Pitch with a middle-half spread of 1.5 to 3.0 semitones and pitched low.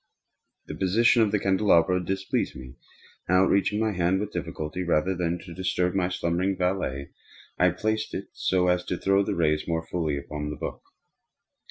Yes: narrow, 2.6 semitones; very low, 90 Hz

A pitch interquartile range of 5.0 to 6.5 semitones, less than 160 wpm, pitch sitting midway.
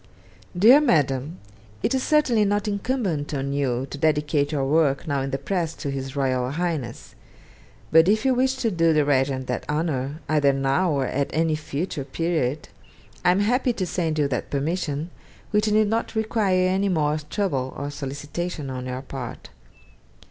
No: wide, 5.4 semitones; average, 170 wpm; medium, 155 Hz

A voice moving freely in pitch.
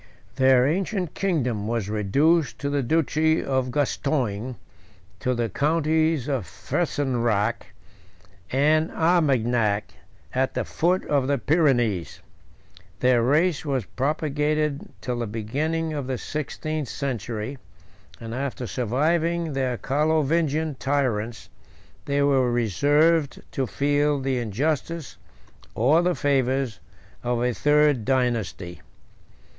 No: average, 4.2 semitones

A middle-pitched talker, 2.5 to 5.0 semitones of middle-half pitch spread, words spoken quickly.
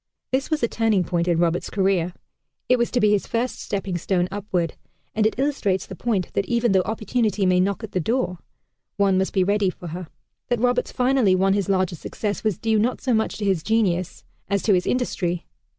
No: high, 200 Hz; average, 3.8 semitones; fast, 215 wpm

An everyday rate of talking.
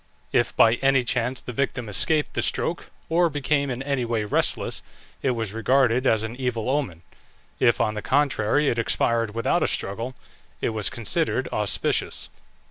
Yes: average, 165 wpm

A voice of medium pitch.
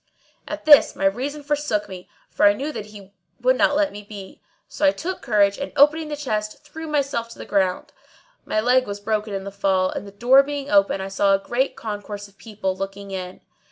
No: high, 210 Hz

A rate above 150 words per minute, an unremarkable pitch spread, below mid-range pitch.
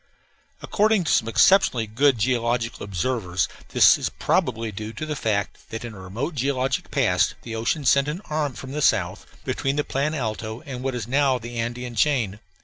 Yes: average, 190 wpm; average, 4.0 semitones; low, 125 Hz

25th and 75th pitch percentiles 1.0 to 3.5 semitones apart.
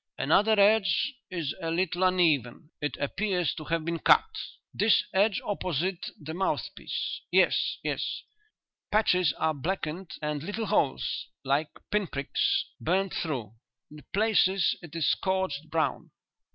No: average, 4.0 semitones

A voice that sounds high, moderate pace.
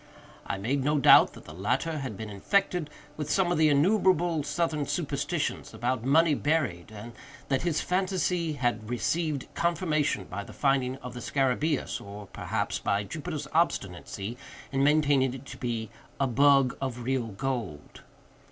No: low, 135 Hz; average, 155 wpm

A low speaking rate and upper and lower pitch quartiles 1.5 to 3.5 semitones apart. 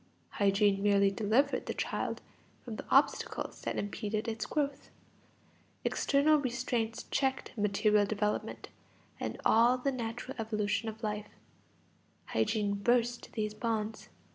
Yes: slow, 115 wpm; average, 2.7 semitones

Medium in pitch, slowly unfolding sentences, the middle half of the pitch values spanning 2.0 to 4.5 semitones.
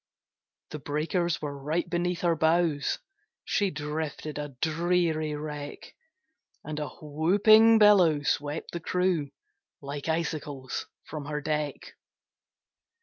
Yes: medium, 155 Hz; slow, 110 wpm; average, 2.7 semitones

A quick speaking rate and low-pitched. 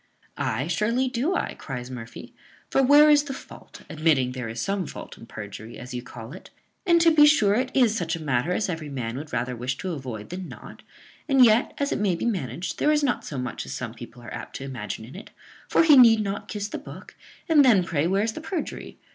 No: fast, 235 wpm; medium, 175 Hz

